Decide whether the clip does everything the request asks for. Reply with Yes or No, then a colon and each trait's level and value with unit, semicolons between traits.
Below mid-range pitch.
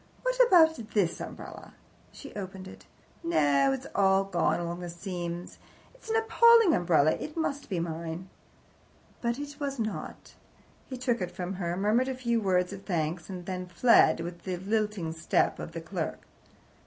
No: high, 190 Hz